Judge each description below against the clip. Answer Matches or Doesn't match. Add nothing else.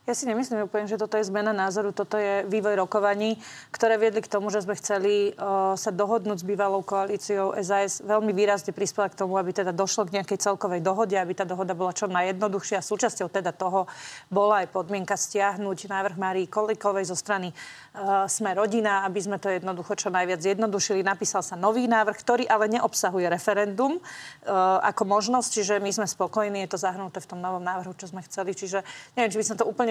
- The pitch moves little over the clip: Matches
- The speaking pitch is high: Matches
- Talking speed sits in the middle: Doesn't match